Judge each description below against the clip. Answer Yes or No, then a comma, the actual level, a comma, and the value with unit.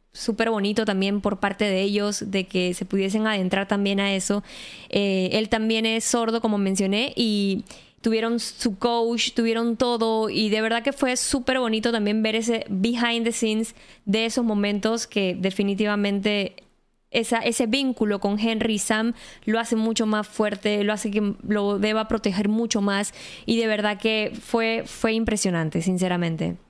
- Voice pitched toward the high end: Yes, high, 215 Hz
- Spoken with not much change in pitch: Yes, narrow, 2.1 semitones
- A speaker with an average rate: Yes, average, 165 wpm